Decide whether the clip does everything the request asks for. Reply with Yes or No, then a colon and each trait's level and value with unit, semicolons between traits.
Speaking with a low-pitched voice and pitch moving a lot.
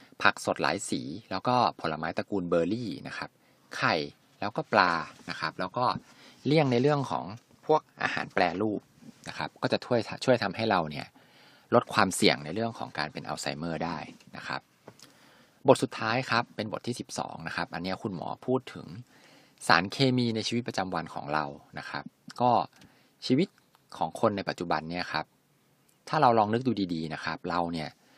Yes: low, 100 Hz; wide, 6.1 semitones